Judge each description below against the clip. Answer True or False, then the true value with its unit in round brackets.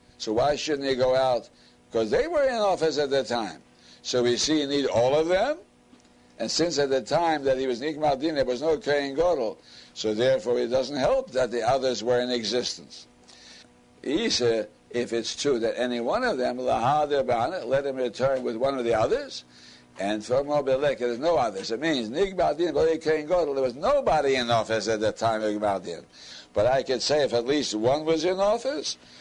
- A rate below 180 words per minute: False (195 wpm)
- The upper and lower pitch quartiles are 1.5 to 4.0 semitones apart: False (5.4 semitones)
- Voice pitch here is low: True (130 Hz)